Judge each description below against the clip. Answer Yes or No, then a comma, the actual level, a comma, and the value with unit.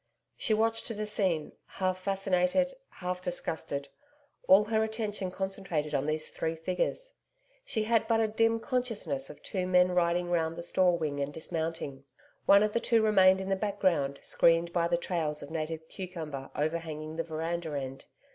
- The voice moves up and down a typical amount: Yes, average, 4.2 semitones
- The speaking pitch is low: No, medium, 180 Hz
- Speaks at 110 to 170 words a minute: Yes, average, 165 wpm